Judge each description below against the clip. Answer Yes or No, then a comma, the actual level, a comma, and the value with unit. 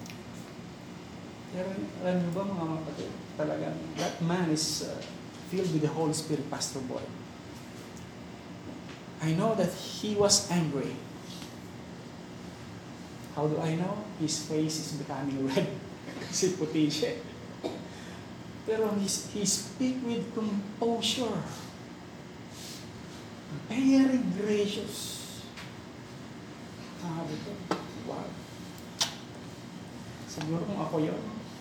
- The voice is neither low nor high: Yes, medium, 155 Hz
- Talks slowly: Yes, slow, 95 wpm